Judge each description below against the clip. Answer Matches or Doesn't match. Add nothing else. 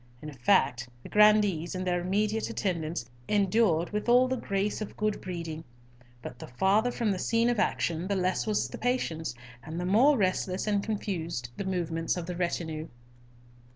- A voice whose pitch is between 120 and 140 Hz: Doesn't match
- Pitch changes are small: Doesn't match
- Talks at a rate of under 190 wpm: Matches